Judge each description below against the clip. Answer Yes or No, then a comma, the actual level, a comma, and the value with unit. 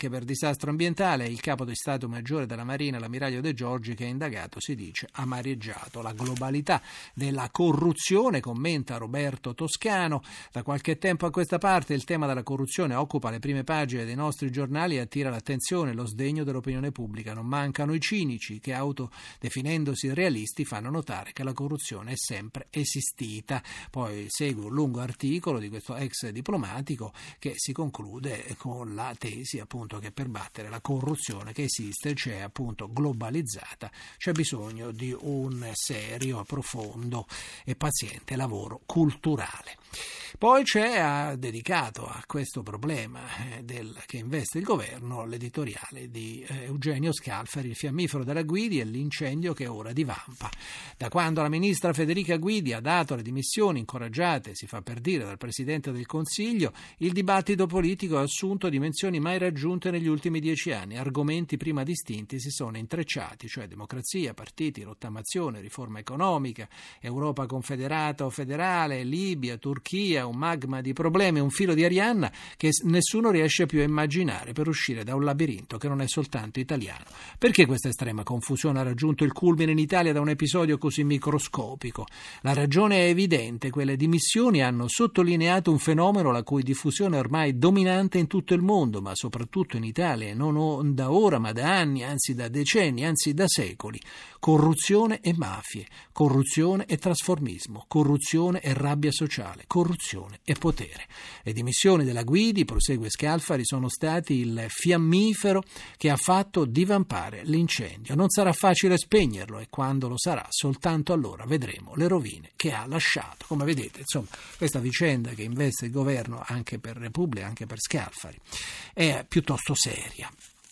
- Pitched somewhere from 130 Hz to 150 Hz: Yes, medium, 140 Hz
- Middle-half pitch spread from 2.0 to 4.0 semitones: No, average, 4.9 semitones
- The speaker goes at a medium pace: Yes, average, 155 wpm